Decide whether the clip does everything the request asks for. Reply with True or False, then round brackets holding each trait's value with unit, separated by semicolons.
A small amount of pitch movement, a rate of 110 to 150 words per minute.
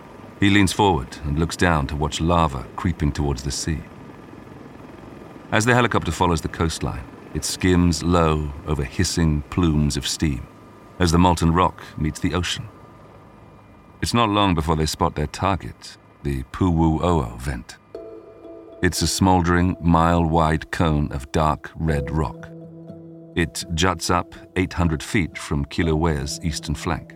False (3.3 semitones; 140 wpm)